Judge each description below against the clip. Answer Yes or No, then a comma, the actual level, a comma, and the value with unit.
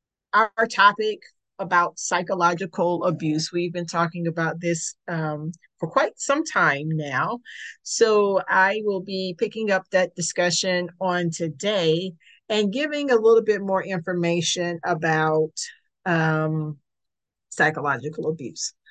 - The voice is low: No, medium, 175 Hz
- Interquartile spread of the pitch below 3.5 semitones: No, average, 4.1 semitones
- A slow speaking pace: Yes, slow, 115 wpm